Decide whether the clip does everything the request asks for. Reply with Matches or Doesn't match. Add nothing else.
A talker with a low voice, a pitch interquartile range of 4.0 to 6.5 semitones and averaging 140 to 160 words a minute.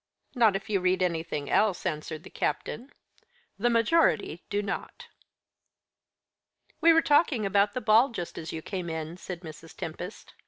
Doesn't match